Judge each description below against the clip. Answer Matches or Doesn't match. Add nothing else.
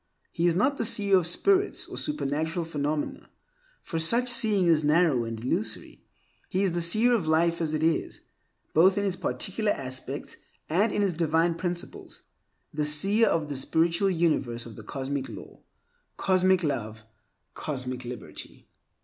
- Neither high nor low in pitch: Matches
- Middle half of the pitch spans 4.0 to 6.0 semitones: Matches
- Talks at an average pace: Matches